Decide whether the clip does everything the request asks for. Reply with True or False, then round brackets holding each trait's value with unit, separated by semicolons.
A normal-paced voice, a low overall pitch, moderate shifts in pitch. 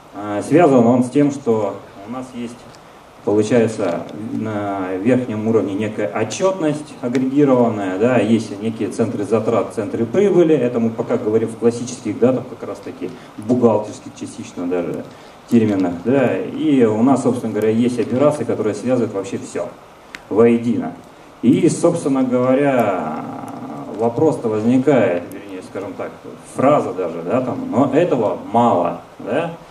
True (130 wpm; 115 Hz; 3.3 semitones)